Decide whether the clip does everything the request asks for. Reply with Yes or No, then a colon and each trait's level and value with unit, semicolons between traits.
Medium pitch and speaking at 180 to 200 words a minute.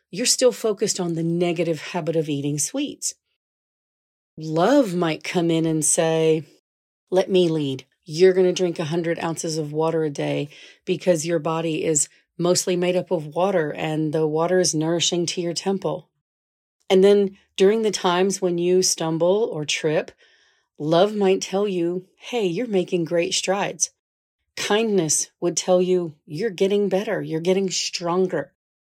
No: medium, 175 Hz; average, 155 wpm